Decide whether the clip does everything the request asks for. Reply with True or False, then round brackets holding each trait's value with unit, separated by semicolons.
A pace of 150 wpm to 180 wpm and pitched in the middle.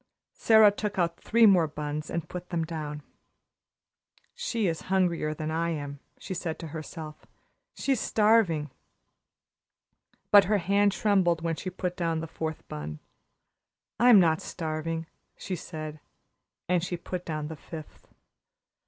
False (140 wpm; 170 Hz)